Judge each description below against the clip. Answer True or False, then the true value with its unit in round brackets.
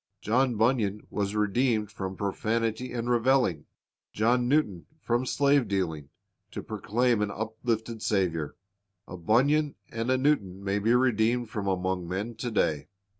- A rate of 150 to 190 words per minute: False (140 wpm)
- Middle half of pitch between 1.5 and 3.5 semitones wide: False (3.9 semitones)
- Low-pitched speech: True (110 Hz)